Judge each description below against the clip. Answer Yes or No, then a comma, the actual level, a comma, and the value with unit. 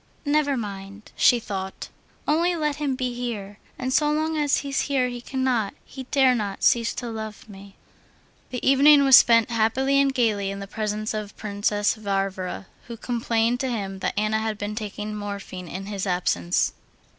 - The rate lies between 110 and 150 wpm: No, average, 175 wpm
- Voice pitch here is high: Yes, high, 225 Hz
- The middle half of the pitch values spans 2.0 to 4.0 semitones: No, average, 4.5 semitones